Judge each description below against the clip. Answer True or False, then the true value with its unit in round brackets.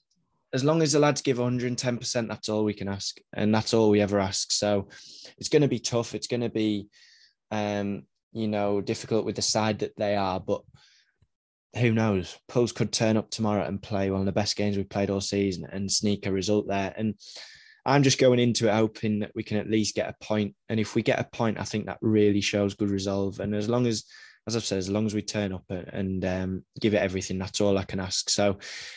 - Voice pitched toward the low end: True (105 Hz)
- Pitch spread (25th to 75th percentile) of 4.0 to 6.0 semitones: False (2.4 semitones)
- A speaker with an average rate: False (240 wpm)